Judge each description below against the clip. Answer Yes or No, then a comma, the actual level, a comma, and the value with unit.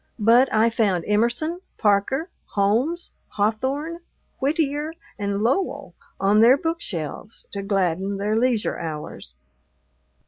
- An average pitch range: No, wide, 5.9 semitones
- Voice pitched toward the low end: No, high, 225 Hz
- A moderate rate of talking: No, slow, 105 wpm